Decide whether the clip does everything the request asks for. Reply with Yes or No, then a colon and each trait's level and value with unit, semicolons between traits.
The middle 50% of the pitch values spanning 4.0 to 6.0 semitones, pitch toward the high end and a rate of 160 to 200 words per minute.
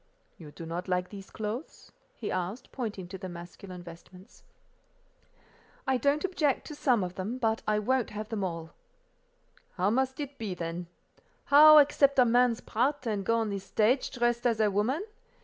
Yes: wide, 5.6 semitones; high, 220 Hz; average, 175 wpm